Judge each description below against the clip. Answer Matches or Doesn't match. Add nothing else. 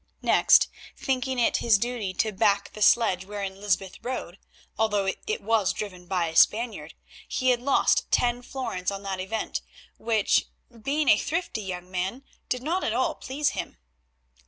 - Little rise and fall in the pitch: Doesn't match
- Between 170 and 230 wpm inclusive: Doesn't match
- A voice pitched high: Matches